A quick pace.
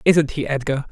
No: average, 195 wpm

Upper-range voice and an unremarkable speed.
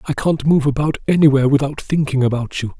No: medium, 140 Hz; average, 195 wpm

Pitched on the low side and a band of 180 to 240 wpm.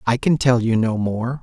No: low, 120 Hz; fast, 255 wpm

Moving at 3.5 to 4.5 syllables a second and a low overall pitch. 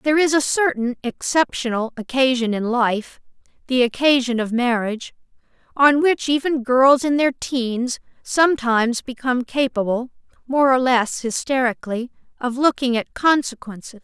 No: 4.4 syllables/s; very high, 255 Hz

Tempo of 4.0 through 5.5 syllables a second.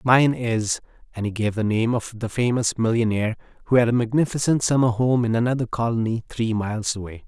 No: 5.8 syllables/s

